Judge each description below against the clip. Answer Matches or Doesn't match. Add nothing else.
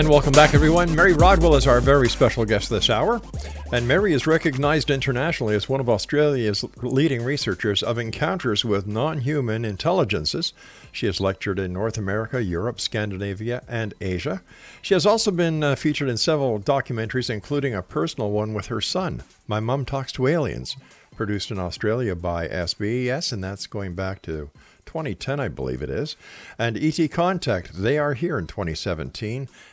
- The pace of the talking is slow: Doesn't match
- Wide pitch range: Matches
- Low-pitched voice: Matches